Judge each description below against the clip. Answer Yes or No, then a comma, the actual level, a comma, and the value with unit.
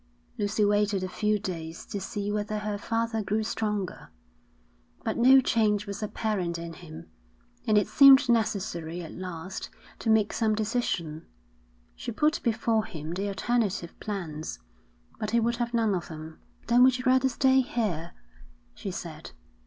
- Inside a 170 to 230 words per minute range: No, average, 155 wpm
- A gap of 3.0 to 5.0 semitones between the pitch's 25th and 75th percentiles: Yes, average, 4.1 semitones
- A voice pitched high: Yes, high, 210 Hz